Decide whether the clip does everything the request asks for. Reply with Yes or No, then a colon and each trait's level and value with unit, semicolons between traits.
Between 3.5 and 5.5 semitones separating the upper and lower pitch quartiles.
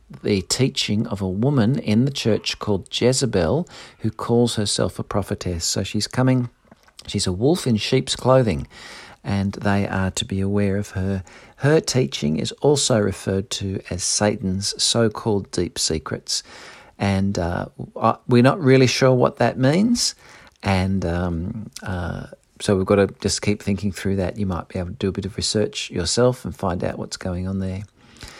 Yes: average, 4.2 semitones